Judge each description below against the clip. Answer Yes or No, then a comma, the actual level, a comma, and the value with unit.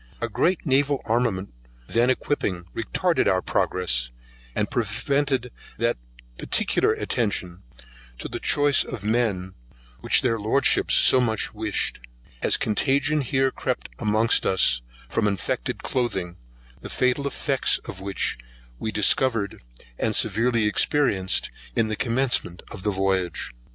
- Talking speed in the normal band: No, slow, 125 wpm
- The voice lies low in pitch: Yes, low, 115 Hz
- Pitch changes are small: No, average, 5.2 semitones